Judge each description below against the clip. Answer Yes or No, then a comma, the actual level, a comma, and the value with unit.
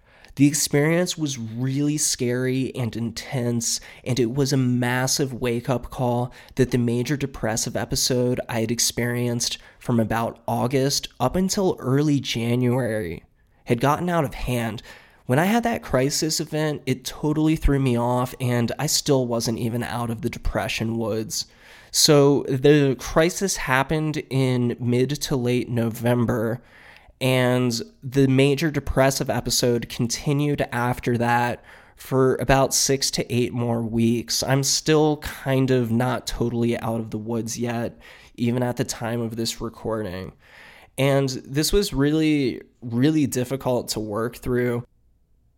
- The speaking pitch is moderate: No, low, 125 Hz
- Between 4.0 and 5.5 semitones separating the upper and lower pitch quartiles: No, average, 2.7 semitones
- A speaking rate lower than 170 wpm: Yes, average, 140 wpm